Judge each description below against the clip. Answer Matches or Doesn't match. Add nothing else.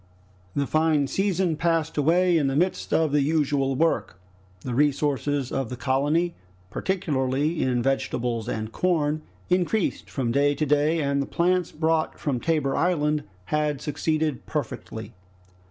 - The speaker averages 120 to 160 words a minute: Matches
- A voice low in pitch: Doesn't match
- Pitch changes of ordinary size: Matches